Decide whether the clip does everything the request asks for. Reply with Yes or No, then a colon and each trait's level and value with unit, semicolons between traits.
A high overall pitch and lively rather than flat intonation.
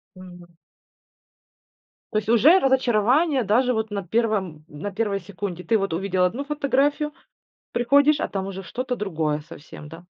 Yes: high, 210 Hz; wide, 5.9 semitones